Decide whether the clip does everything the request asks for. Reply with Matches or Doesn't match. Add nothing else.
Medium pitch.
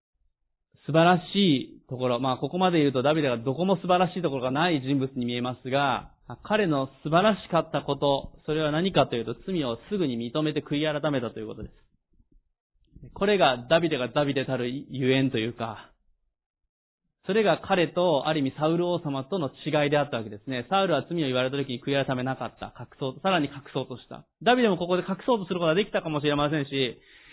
Matches